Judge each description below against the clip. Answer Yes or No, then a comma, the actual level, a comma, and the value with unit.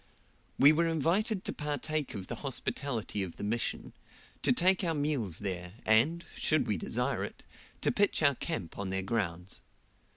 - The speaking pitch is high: No, low, 135 Hz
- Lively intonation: Yes, wide, 7.9 semitones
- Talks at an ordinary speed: Yes, average, 165 wpm